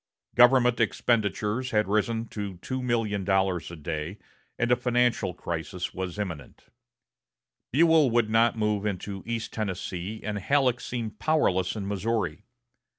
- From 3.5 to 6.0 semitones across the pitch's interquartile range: Yes, average, 3.9 semitones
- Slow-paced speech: Yes, slow, 125 wpm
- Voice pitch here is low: Yes, low, 105 Hz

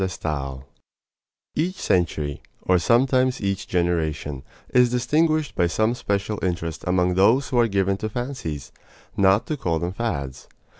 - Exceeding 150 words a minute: No, average, 145 wpm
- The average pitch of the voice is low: Yes, very low, 95 Hz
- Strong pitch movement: Yes, wide, 6.6 semitones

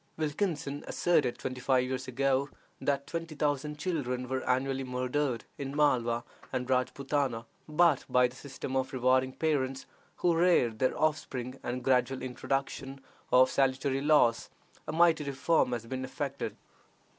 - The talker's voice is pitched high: No, low, 135 Hz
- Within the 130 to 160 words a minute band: Yes, average, 145 wpm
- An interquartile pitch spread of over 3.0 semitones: No, narrow, 2.5 semitones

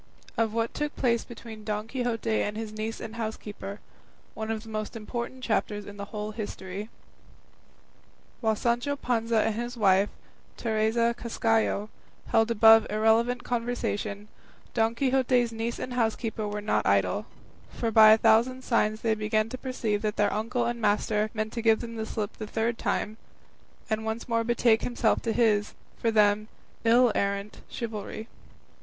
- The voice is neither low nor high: No, high, 225 Hz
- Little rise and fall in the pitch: Yes, narrow, 1.7 semitones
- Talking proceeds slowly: No, average, 160 wpm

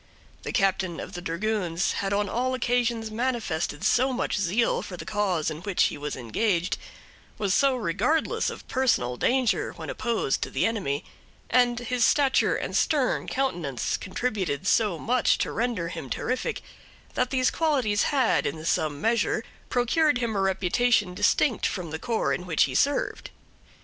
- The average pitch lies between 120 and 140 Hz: No, high, 215 Hz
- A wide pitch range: Yes, wide, 5.7 semitones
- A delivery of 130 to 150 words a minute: No, average, 160 wpm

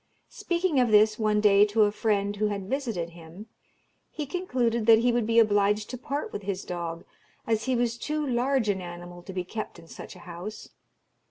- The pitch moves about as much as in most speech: Yes, average, 3.9 semitones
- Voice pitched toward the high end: Yes, high, 215 Hz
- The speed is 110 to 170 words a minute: No, average, 200 wpm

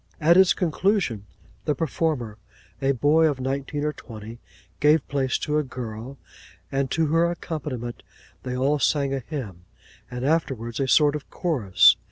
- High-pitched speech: No, medium, 140 Hz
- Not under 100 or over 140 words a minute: No, average, 155 wpm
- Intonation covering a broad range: No, average, 3.8 semitones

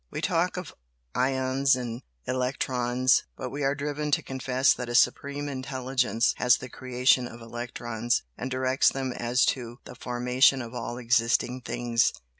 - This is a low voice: Yes, low, 125 Hz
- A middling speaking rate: Yes, average, 155 wpm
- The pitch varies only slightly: Yes, narrow, 1.5 semitones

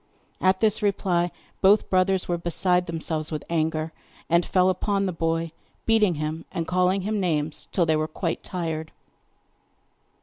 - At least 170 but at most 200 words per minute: No, average, 155 wpm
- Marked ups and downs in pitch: No, narrow, 2.6 semitones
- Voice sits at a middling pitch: Yes, medium, 175 Hz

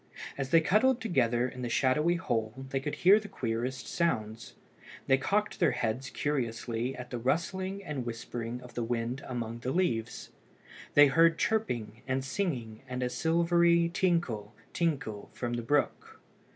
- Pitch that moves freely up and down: Yes, wide, 6.1 semitones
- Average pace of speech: Yes, average, 155 wpm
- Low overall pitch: Yes, low, 130 Hz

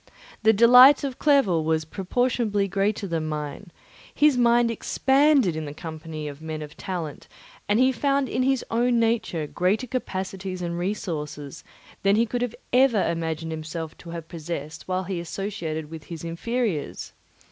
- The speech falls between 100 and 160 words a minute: Yes, average, 155 wpm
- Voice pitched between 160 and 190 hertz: Yes, medium, 185 Hz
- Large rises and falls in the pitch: Yes, wide, 6.7 semitones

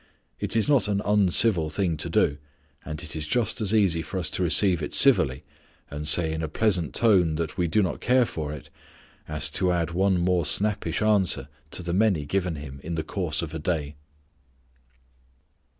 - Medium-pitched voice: No, very low, 85 Hz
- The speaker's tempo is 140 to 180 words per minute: No, average, 195 wpm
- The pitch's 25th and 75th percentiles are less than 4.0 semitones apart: No, average, 4.3 semitones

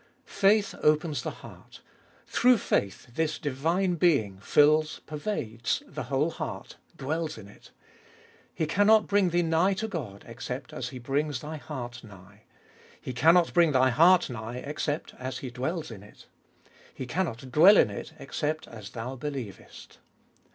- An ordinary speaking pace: Yes, average, 155 wpm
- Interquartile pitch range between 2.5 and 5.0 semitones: No, wide, 5.6 semitones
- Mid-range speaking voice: Yes, medium, 145 Hz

